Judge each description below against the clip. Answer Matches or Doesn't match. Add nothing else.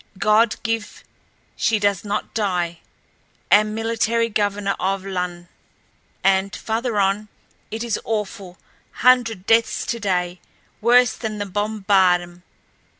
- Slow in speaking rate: Matches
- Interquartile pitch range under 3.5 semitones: Matches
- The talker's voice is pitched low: Doesn't match